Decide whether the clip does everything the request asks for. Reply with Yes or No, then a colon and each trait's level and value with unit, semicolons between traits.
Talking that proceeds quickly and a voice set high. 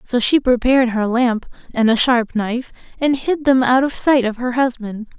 Yes: fast, 210 wpm; high, 245 Hz